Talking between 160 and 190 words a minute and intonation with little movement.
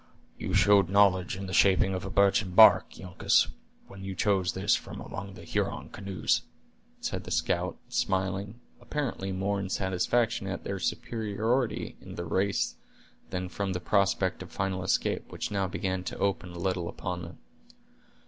Yes: average, 165 wpm; narrow, 1.4 semitones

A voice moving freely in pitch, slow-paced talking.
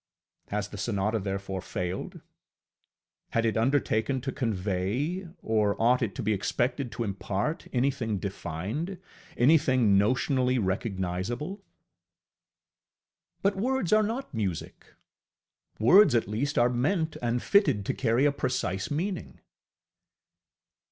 Yes: wide, 6.1 semitones; slow, 115 wpm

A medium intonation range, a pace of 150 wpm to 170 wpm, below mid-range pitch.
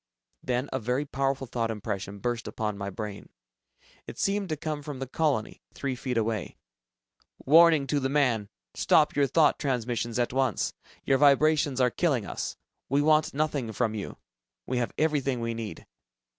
Yes: average, 4.1 semitones; average, 165 wpm; low, 130 Hz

